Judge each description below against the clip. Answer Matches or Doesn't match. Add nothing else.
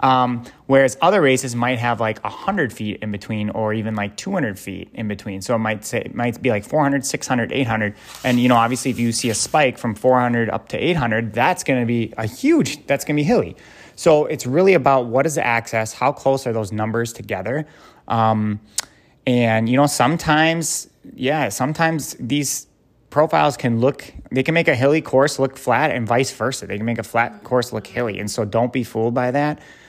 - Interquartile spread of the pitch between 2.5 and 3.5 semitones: Doesn't match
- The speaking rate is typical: Doesn't match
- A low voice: Matches